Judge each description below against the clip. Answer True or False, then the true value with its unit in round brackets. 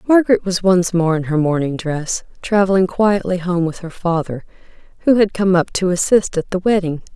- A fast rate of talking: False (195 wpm)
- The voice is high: False (180 Hz)